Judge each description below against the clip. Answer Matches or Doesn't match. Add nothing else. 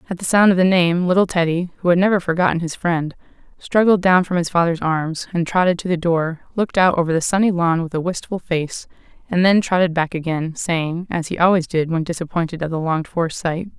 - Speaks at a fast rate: Matches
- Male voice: Doesn't match